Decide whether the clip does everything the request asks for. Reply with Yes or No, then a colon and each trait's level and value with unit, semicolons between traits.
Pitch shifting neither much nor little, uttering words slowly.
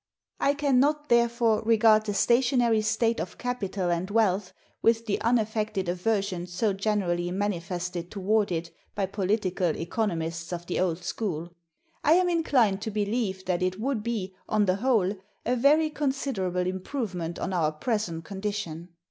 No: average, 4.2 semitones; average, 150 wpm